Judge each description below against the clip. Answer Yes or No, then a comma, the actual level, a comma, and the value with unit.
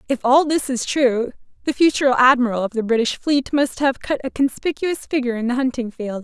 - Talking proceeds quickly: Yes, fast, 210 wpm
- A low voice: No, very high, 255 Hz